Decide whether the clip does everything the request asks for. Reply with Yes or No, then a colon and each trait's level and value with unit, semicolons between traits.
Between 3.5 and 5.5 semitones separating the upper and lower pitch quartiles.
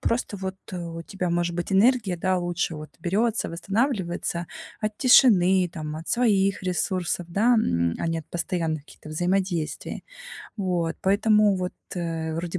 No: average, 2.8 semitones